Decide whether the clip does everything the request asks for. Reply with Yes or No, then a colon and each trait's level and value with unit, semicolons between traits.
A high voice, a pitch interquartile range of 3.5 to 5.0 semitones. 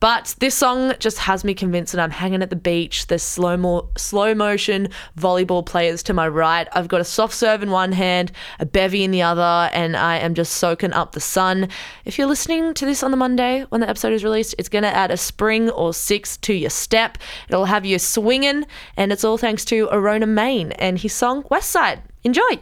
Yes: high, 195 Hz; average, 4.2 semitones